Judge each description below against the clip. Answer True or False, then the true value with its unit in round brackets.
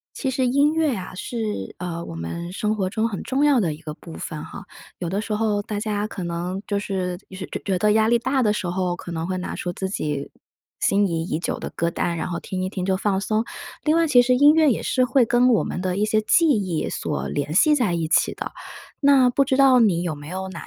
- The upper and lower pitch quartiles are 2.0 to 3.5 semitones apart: False (5.6 semitones)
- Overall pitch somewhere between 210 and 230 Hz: False (200 Hz)